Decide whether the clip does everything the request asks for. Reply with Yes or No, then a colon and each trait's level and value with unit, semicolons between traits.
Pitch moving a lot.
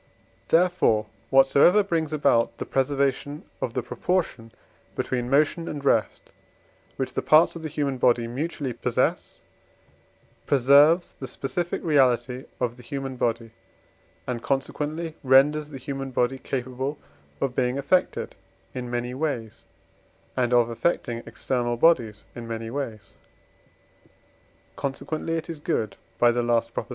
No: average, 3.7 semitones